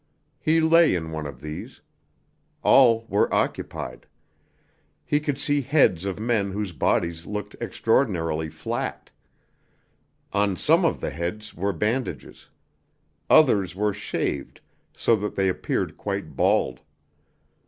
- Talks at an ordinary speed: No, slow, 120 wpm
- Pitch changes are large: Yes, wide, 5.7 semitones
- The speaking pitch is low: Yes, low, 105 Hz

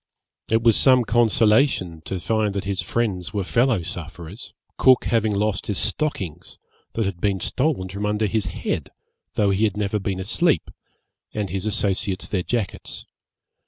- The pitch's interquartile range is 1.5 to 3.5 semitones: Yes, average, 3.0 semitones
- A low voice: Yes, low, 105 Hz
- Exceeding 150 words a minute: Yes, average, 160 wpm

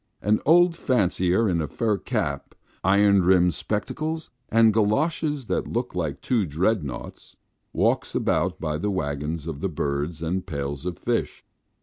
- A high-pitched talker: No, very low, 95 Hz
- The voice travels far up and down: Yes, wide, 6.2 semitones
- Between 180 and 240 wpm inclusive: No, average, 145 wpm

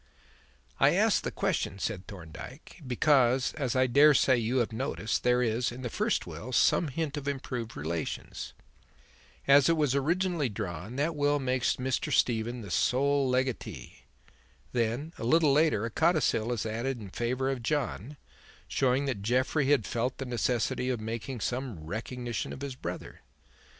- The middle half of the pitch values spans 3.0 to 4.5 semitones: Yes, average, 3.4 semitones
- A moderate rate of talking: Yes, average, 160 wpm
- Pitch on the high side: No, low, 125 Hz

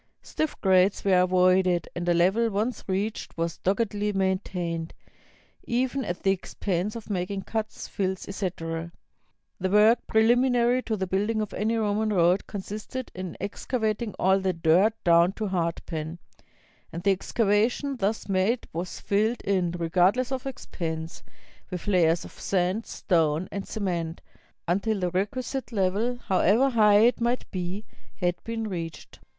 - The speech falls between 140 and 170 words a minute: Yes, average, 145 wpm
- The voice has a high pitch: Yes, high, 195 Hz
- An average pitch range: Yes, average, 3.6 semitones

